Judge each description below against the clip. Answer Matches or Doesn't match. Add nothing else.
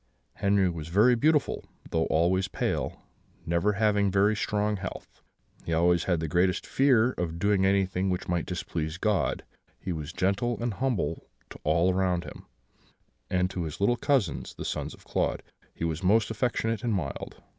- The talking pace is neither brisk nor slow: Matches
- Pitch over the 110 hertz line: Doesn't match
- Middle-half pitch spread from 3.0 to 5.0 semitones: Matches